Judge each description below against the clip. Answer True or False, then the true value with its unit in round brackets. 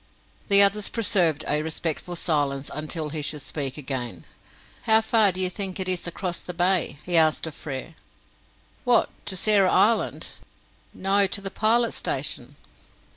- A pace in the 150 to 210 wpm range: True (155 wpm)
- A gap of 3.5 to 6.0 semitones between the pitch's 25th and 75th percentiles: True (4.7 semitones)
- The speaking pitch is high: False (180 Hz)